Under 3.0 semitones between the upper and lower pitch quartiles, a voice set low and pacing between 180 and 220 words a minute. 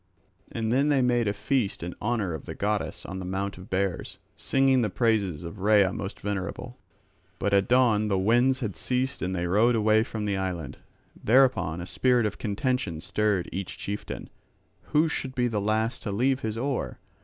No: average, 4.3 semitones; low, 105 Hz; average, 190 wpm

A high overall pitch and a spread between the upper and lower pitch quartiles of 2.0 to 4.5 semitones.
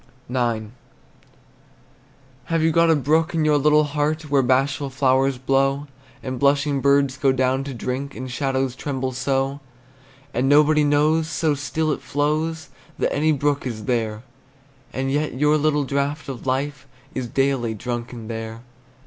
No: medium, 140 Hz; narrow, 2.4 semitones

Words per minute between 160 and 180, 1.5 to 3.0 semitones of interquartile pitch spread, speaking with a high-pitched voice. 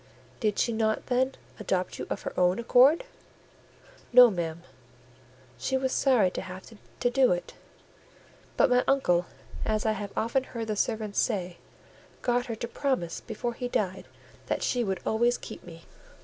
No: average, 165 wpm; average, 4.6 semitones; high, 220 Hz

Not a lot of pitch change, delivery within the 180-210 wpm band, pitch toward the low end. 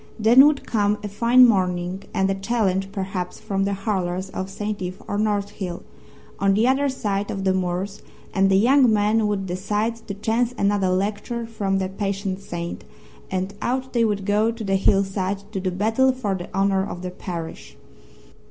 No: narrow, 2.3 semitones; average, 185 wpm; high, 200 Hz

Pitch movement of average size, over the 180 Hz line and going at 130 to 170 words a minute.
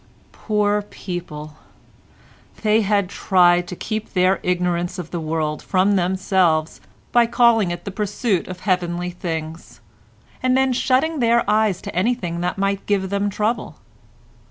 Yes: average, 3.3 semitones; high, 190 Hz; average, 140 wpm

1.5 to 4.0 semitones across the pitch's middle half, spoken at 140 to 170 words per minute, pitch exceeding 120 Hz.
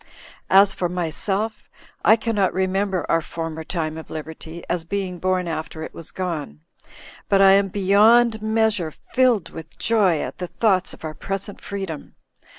Yes: average, 3.7 semitones; average, 155 wpm; medium, 185 Hz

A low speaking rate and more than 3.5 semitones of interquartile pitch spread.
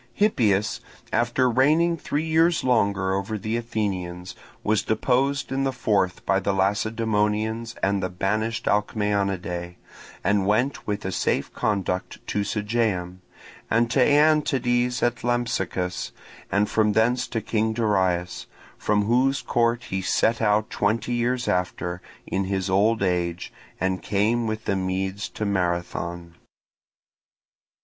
Yes: slow, 130 wpm; average, 3.9 semitones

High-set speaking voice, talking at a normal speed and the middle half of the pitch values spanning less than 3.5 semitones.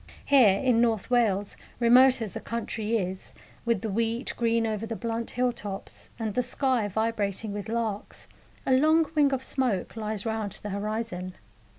Yes: high, 225 Hz; average, 170 wpm; average, 2.7 semitones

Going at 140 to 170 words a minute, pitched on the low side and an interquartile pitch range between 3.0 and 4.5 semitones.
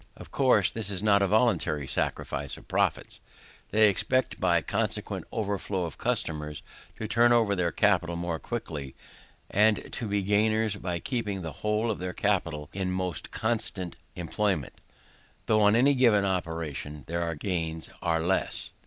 Yes: average, 155 wpm; very low, 95 Hz; average, 4.2 semitones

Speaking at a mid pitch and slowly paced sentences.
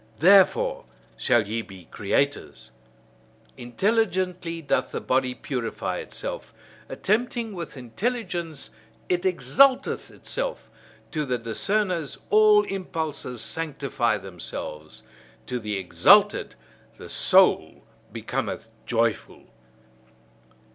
Yes: medium, 150 Hz; slow, 90 wpm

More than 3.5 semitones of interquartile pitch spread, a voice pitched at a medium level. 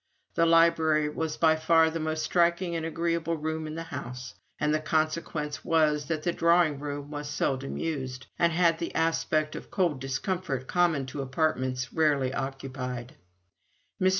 No: average, 3.1 semitones; medium, 155 Hz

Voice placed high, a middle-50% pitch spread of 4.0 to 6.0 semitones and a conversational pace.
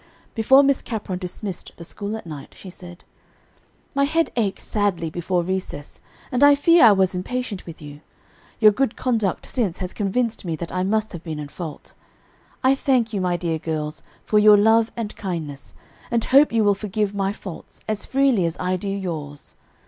Yes: high, 200 Hz; average, 4.6 semitones; average, 185 wpm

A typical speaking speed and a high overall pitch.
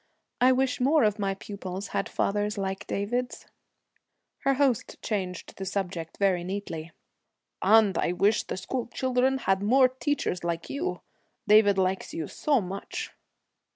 Yes: average, 145 wpm; high, 205 Hz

